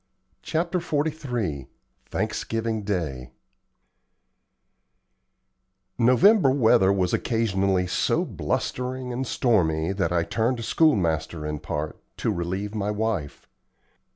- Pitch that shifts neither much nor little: No, wide, 6.6 semitones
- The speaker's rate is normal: No, slow, 95 wpm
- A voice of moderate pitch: No, low, 105 Hz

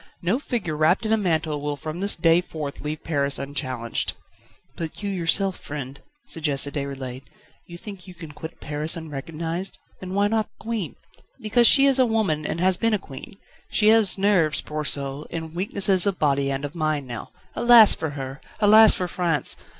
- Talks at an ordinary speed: Yes, average, 185 wpm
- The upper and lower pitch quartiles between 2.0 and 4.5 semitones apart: No, wide, 5.4 semitones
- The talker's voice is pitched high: No, medium, 165 Hz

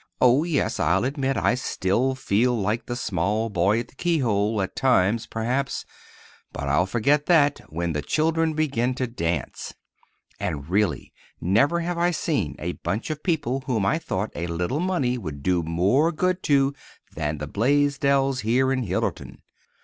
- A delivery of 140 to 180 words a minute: Yes, average, 160 wpm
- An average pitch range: No, wide, 7.0 semitones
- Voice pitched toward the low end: Yes, low, 120 Hz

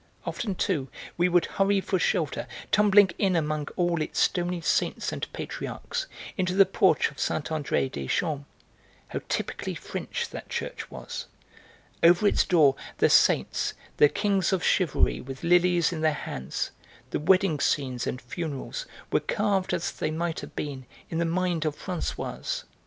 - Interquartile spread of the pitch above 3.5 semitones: Yes, average, 3.9 semitones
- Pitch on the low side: No, medium, 170 Hz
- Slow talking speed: No, average, 160 wpm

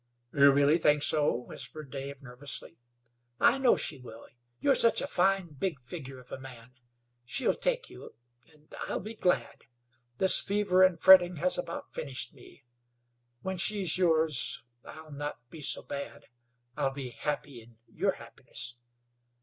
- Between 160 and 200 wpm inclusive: No, average, 150 wpm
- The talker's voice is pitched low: No, medium, 150 Hz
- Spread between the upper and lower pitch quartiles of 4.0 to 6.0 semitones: Yes, average, 5.3 semitones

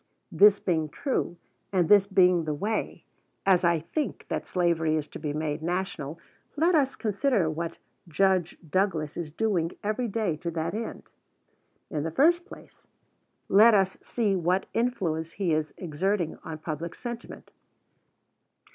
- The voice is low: No, medium, 180 Hz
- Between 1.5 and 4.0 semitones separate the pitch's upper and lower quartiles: No, average, 4.6 semitones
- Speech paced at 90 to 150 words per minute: Yes, average, 145 wpm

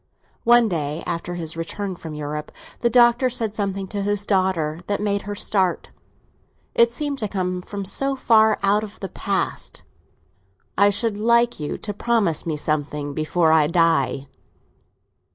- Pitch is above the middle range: Yes, high, 195 Hz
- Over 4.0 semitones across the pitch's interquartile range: Yes, average, 4.8 semitones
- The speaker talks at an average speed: Yes, average, 155 wpm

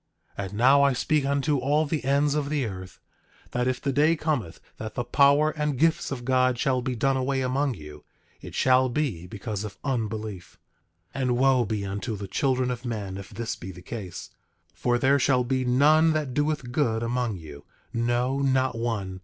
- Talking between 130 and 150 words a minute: No, average, 195 wpm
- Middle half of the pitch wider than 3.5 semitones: Yes, average, 4.1 semitones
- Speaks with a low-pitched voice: Yes, low, 125 Hz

